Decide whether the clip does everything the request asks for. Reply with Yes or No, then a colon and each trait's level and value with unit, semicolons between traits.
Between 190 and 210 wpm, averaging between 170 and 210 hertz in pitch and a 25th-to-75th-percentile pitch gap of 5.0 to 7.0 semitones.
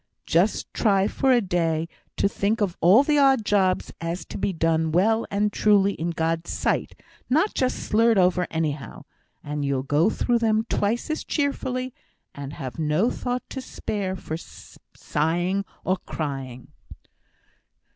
No: average, 155 wpm; high, 190 Hz; wide, 5.6 semitones